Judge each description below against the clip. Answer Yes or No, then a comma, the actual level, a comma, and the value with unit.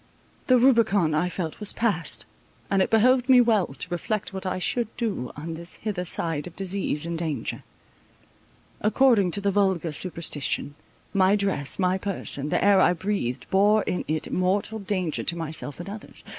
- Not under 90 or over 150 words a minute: No, average, 170 wpm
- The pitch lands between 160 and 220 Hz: Yes, high, 190 Hz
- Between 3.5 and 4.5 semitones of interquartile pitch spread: Yes, average, 3.9 semitones